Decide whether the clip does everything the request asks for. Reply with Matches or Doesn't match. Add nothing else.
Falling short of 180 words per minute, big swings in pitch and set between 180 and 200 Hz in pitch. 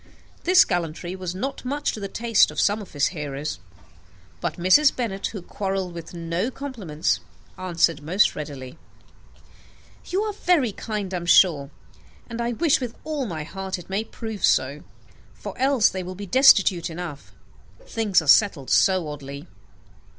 Matches